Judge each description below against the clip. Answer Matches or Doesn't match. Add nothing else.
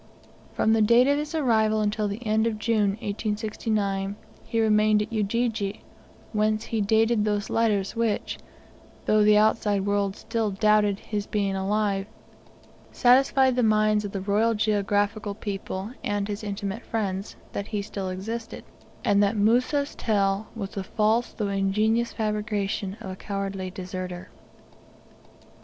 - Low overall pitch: Doesn't match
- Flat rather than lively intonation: Matches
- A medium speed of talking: Matches